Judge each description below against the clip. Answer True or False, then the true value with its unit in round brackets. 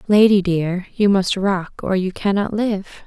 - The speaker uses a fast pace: False (175 wpm)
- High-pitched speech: True (195 Hz)